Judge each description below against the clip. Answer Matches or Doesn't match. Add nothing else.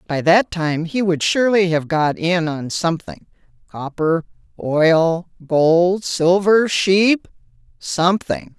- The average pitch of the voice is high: Doesn't match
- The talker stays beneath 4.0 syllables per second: Matches